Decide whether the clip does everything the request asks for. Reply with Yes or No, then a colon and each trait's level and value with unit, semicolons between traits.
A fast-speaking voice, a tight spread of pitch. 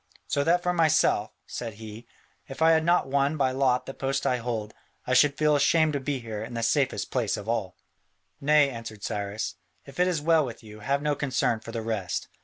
No: fast, 215 wpm; average, 4.6 semitones